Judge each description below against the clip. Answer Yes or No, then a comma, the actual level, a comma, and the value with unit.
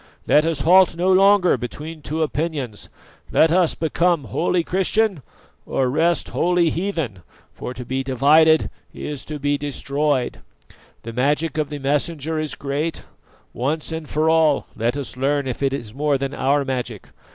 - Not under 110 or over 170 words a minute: Yes, average, 160 wpm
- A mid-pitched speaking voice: Yes, medium, 150 Hz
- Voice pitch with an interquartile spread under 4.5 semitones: Yes, average, 3.2 semitones